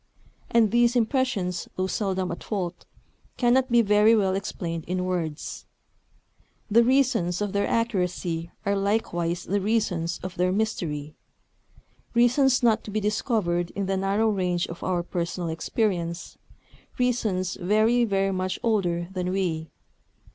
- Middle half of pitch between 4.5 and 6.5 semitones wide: No, average, 3.9 semitones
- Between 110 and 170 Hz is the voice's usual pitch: No, high, 195 Hz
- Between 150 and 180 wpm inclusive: No, slow, 135 wpm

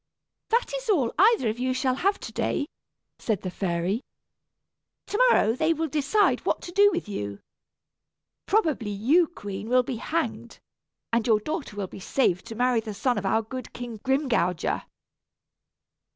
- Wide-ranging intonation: Yes, wide, 7.4 semitones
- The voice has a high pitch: Yes, very high, 250 Hz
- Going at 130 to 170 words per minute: Yes, average, 160 wpm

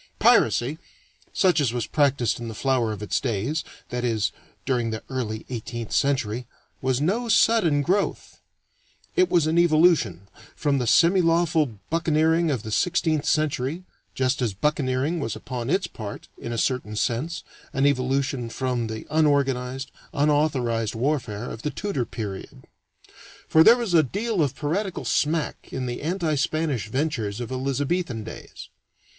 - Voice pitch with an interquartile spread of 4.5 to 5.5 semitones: Yes, average, 5.1 semitones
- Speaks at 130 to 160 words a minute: Yes, average, 150 wpm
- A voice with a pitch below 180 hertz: Yes, low, 135 Hz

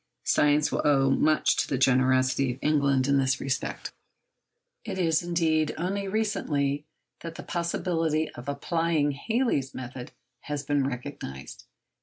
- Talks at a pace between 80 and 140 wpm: Yes, slow, 135 wpm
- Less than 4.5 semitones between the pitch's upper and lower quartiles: Yes, average, 3.5 semitones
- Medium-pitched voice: Yes, medium, 145 Hz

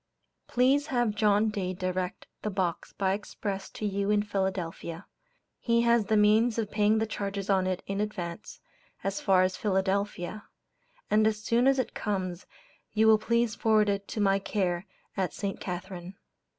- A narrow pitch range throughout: Yes, narrow, 2.3 semitones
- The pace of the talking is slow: No, average, 170 wpm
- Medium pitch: No, high, 205 Hz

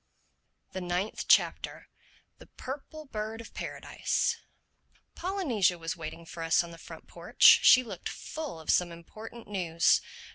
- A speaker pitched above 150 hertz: Yes, high, 190 Hz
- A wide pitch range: Yes, wide, 6.1 semitones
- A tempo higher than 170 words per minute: No, average, 140 wpm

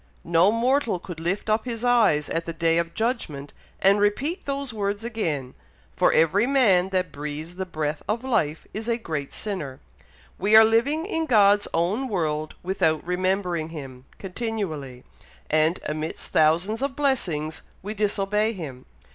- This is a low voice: No, high, 190 Hz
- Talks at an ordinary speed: Yes, average, 155 wpm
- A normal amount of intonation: No, wide, 6.0 semitones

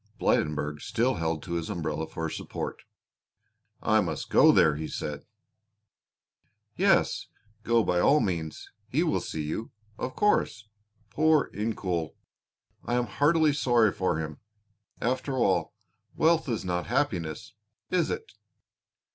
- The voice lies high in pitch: No, low, 105 Hz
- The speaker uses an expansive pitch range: Yes, wide, 8.1 semitones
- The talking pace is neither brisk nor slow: No, slow, 130 wpm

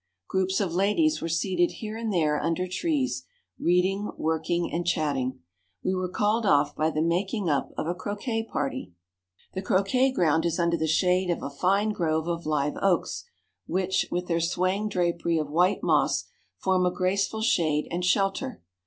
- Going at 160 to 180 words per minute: Yes, average, 170 wpm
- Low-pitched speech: No, medium, 180 Hz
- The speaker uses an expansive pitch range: No, average, 3.2 semitones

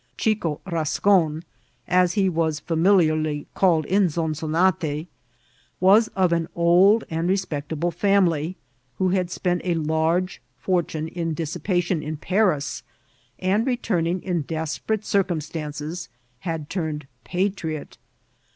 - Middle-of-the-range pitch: Yes, medium, 170 Hz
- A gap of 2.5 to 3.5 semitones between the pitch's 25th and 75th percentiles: Yes, average, 3.0 semitones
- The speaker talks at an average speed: No, slow, 115 wpm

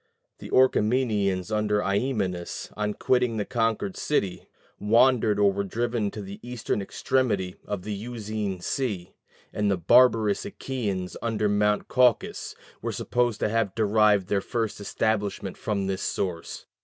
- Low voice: Yes, low, 105 Hz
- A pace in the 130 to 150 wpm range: Yes, average, 140 wpm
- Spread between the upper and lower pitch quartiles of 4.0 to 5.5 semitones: No, average, 2.8 semitones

